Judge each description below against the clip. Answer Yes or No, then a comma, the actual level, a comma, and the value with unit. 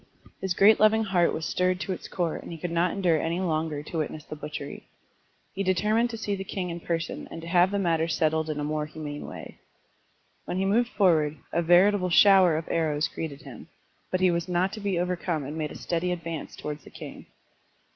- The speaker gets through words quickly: Yes, fast, 220 wpm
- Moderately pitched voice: Yes, medium, 170 Hz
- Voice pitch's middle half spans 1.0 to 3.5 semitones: Yes, average, 3.1 semitones